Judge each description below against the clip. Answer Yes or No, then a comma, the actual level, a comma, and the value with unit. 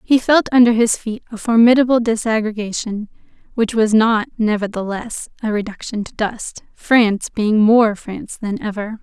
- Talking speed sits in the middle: Yes, average, 145 wpm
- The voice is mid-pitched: No, high, 220 Hz